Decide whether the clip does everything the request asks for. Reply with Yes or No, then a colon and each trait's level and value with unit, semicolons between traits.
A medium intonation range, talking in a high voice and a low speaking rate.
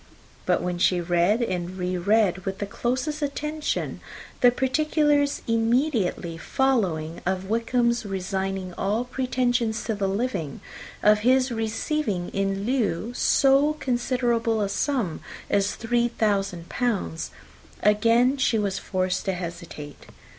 Yes: average, 4.9 semitones; high, 220 Hz; slow, 125 wpm